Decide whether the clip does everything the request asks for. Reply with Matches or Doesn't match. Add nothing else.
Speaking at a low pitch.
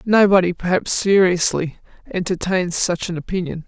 Doesn't match